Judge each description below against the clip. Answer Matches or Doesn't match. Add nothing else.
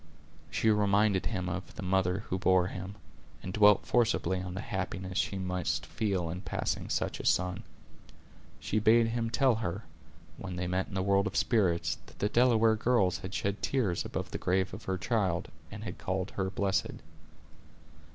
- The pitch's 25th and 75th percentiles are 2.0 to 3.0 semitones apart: Matches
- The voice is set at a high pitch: Doesn't match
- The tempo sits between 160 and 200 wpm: Matches